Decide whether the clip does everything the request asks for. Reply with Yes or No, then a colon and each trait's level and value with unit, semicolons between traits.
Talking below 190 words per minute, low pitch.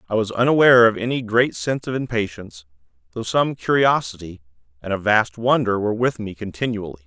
Yes: average, 170 wpm; low, 110 Hz